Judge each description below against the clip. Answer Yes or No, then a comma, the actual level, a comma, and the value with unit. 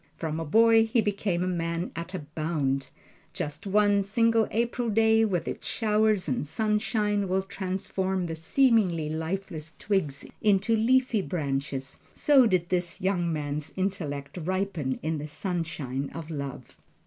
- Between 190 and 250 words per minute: No, average, 150 wpm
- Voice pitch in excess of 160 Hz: Yes, medium, 185 Hz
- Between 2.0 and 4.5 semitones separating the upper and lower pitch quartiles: No, average, 5.1 semitones